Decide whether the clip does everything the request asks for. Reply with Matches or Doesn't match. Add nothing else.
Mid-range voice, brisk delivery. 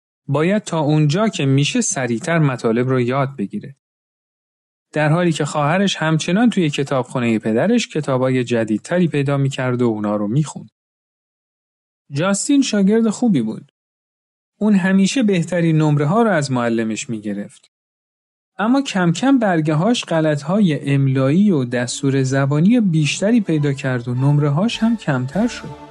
Doesn't match